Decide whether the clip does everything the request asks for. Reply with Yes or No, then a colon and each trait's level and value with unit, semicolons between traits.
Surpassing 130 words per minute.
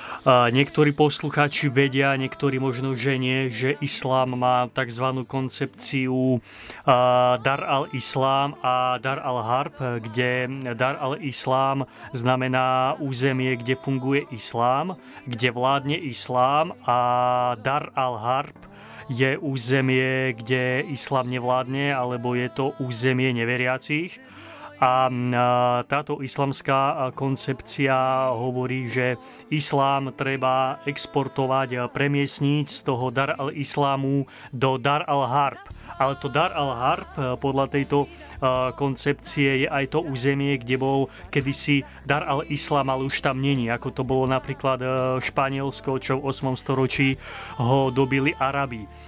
No: average, 115 wpm